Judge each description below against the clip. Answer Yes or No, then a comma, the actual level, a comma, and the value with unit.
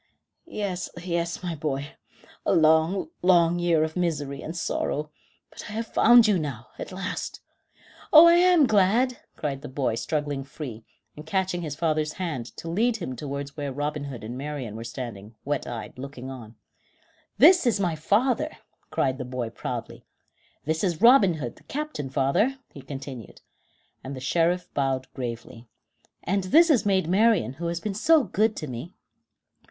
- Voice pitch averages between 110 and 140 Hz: No, medium, 160 Hz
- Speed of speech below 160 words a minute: No, average, 170 wpm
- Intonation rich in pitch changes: Yes, wide, 6.3 semitones